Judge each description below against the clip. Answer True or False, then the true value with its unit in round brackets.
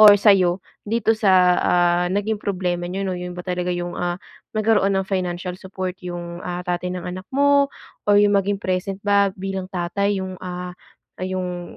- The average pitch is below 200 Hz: True (185 Hz)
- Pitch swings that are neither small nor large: False (2.0 semitones)